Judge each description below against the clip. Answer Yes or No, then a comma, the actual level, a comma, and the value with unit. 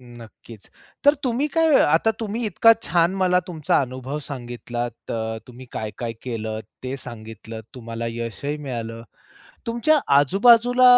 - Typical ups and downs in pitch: No, wide, 9.0 semitones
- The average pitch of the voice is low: Yes, low, 130 Hz